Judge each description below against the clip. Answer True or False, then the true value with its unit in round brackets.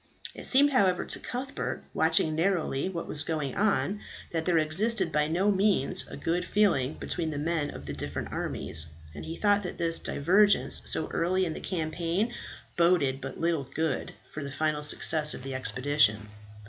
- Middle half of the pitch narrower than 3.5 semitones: False (4.3 semitones)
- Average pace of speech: True (175 wpm)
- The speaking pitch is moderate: True (165 Hz)